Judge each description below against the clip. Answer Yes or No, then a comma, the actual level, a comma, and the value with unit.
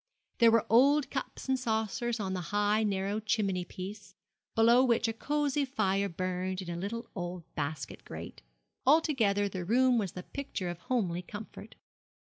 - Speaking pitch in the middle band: No, high, 210 Hz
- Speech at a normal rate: Yes, average, 160 wpm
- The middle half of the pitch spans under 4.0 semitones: No, average, 4.5 semitones